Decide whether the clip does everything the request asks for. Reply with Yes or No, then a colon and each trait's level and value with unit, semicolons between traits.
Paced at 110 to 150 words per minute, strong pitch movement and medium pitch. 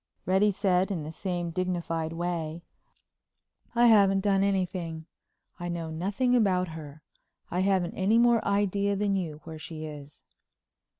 No: average, 140 wpm; average, 3.4 semitones; medium, 180 Hz